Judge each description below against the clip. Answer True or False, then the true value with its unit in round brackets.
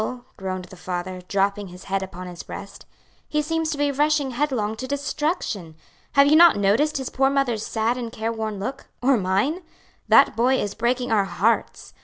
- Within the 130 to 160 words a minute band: False (180 wpm)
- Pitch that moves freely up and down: True (6.2 semitones)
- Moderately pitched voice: False (230 Hz)